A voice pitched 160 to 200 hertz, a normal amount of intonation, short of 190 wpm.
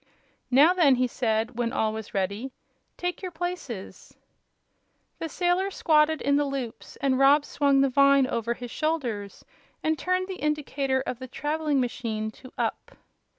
No: very high, 275 Hz; average, 4.5 semitones; average, 155 wpm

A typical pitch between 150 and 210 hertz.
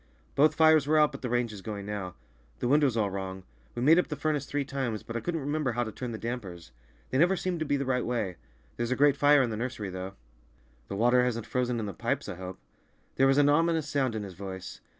No: low, 125 Hz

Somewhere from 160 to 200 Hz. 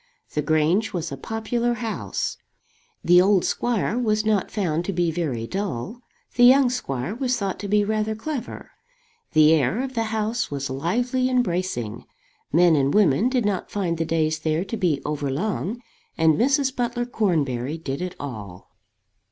Yes: high, 190 Hz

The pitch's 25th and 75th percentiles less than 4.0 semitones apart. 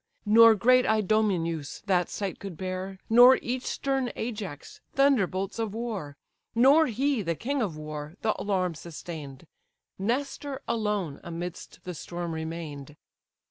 No: wide, 5.6 semitones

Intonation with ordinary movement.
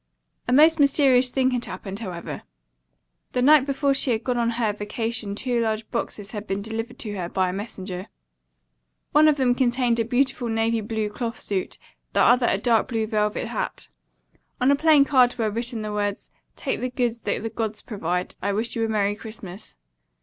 Yes: average, 3.1 semitones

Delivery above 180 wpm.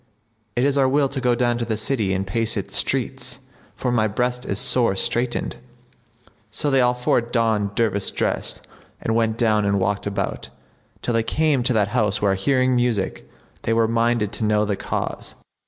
Yes: average, 190 wpm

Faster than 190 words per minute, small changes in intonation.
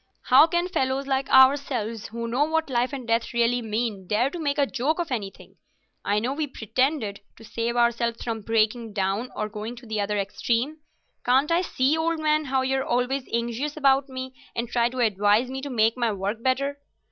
No: fast, 205 wpm; average, 3.4 semitones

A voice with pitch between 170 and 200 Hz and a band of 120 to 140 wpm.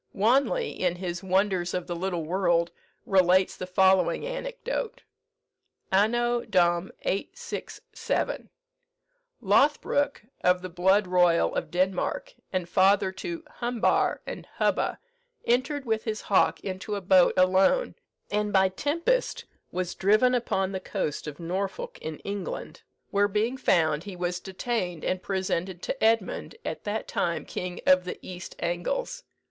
Yes: high, 190 Hz; slow, 135 wpm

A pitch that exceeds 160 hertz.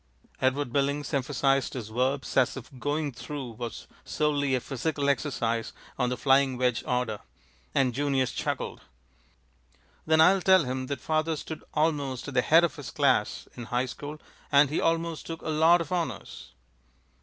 No: medium, 140 Hz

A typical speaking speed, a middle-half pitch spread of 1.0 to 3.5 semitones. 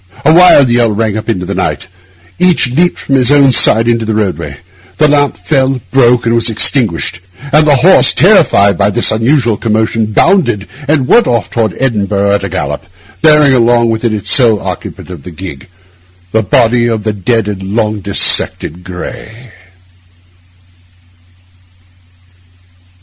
No: average, 155 wpm; average, 4.4 semitones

